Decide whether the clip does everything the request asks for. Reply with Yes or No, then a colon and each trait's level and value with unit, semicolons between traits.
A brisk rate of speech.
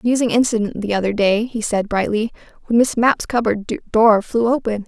No: average, 185 wpm